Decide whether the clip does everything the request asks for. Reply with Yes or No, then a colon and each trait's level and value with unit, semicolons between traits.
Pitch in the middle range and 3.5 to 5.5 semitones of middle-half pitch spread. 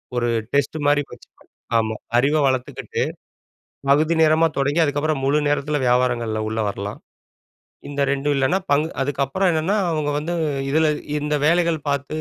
No: medium, 145 Hz; average, 2.7 semitones